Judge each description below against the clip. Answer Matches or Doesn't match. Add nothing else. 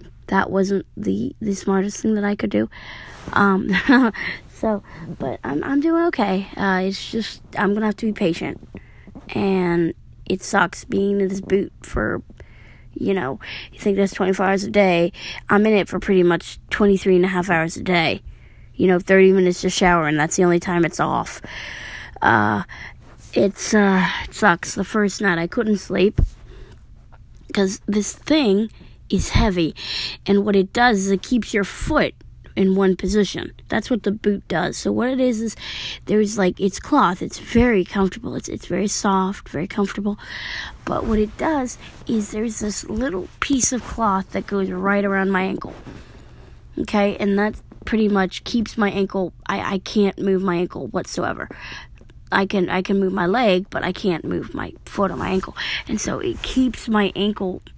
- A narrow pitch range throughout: Matches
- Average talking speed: Matches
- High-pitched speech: Matches